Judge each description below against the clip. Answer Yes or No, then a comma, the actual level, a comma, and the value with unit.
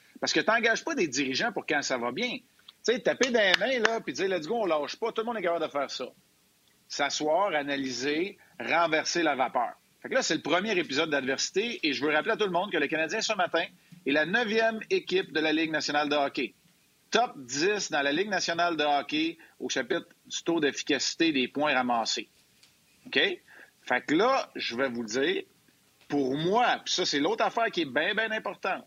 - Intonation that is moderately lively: No, wide, 7.7 semitones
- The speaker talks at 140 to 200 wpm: No, fast, 220 wpm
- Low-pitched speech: No, medium, 170 Hz